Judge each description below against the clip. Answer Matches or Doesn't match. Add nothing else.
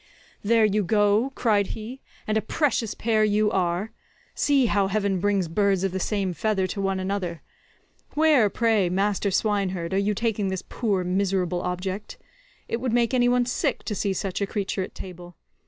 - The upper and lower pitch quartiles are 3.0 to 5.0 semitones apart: Doesn't match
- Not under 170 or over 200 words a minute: Matches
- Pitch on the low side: Doesn't match